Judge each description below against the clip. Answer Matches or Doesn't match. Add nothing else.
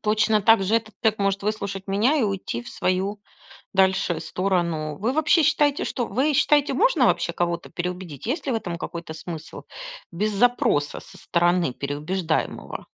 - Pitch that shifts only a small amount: Doesn't match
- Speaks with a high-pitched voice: Matches